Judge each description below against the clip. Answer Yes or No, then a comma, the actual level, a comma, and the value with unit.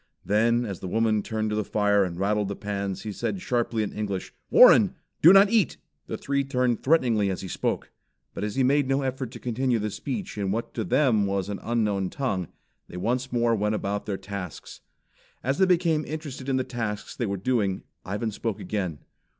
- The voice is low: Yes, low, 110 Hz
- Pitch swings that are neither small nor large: Yes, average, 4.4 semitones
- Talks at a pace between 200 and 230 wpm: Yes, fast, 205 wpm